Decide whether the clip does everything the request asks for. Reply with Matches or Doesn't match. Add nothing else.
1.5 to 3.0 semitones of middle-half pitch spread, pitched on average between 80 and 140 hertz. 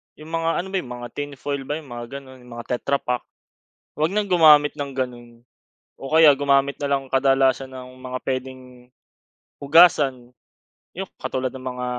Matches